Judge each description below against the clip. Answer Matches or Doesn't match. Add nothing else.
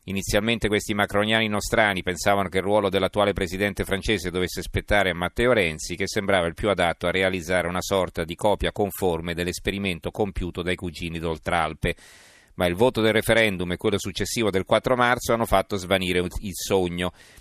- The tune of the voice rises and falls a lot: Doesn't match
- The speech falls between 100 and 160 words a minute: Doesn't match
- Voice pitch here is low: Matches